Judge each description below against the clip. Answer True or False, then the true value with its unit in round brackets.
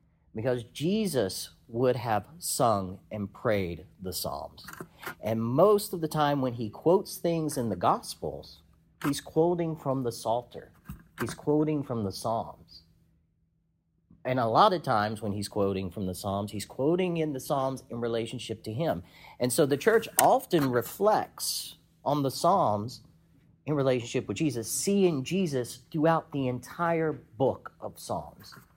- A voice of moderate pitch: False (130 Hz)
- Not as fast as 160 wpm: True (150 wpm)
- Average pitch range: False (5.9 semitones)